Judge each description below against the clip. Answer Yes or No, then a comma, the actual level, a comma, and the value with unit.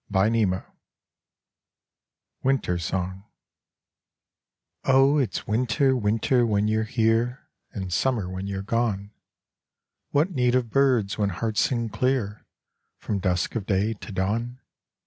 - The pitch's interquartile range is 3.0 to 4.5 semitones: Yes, average, 4.1 semitones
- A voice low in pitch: Yes, low, 110 Hz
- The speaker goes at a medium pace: No, slow, 115 wpm